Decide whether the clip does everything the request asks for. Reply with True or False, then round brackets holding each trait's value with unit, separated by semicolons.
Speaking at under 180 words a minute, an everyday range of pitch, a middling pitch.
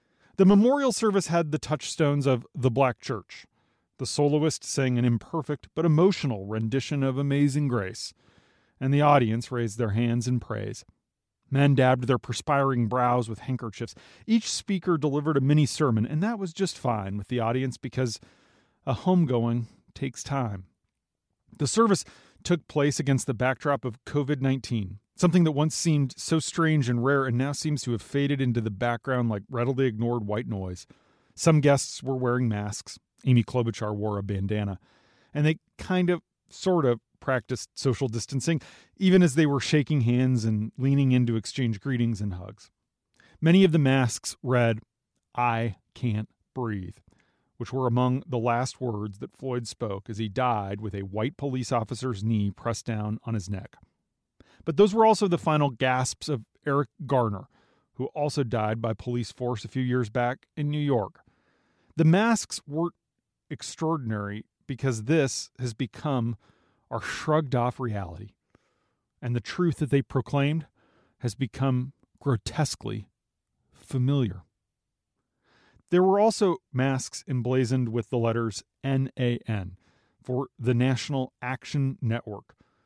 False (150 wpm; 4.0 semitones; 130 Hz)